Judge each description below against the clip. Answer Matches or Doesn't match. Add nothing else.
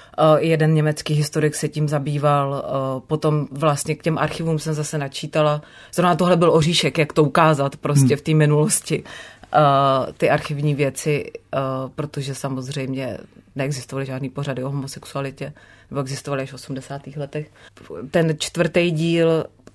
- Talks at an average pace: Matches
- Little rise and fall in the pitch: Matches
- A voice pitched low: Doesn't match